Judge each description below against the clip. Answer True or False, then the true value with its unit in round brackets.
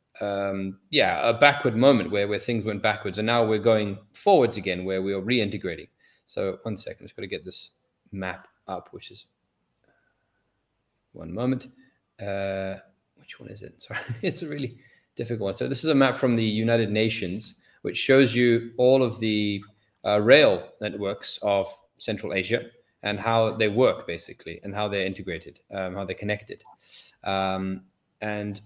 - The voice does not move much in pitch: False (3.3 semitones)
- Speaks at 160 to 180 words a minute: True (165 wpm)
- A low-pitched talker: True (105 Hz)